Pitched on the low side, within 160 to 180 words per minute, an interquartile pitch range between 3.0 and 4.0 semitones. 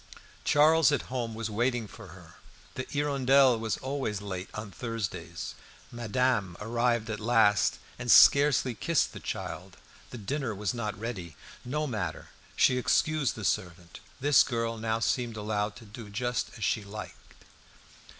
No: low, 115 Hz; average, 150 wpm; average, 3.5 semitones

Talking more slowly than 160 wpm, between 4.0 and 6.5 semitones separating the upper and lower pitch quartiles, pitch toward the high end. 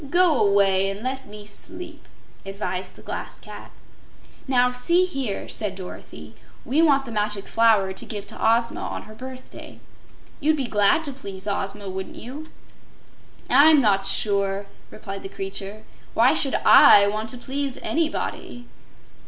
Yes: average, 150 wpm; average, 5.2 semitones; high, 215 Hz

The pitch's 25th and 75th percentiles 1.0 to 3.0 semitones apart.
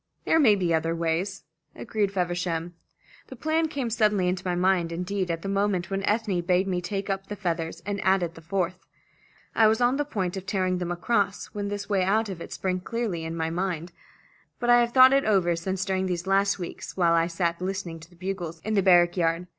Yes: average, 2.7 semitones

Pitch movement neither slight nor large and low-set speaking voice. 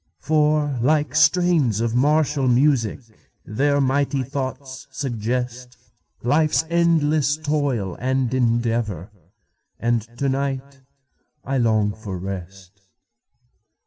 Yes: average, 4.2 semitones; low, 130 Hz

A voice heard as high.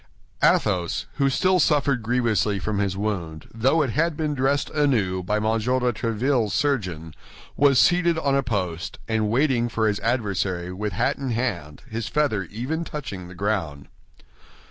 No: low, 115 Hz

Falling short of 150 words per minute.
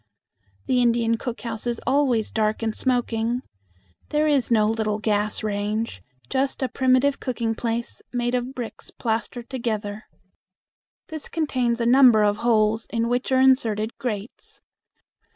Yes: average, 140 wpm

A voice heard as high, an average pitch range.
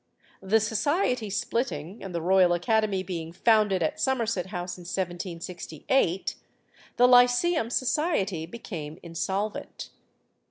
Yes: high, 195 Hz; average, 4.9 semitones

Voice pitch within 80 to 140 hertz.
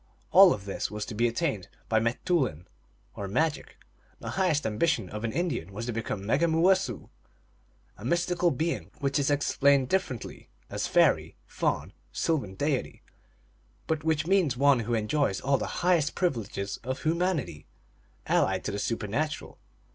Yes: low, 135 Hz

